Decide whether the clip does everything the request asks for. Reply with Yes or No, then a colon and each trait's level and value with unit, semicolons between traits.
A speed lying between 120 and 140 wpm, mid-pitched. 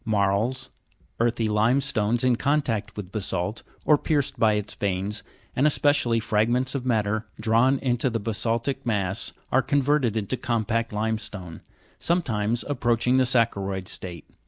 No: slow, 135 wpm; low, 115 Hz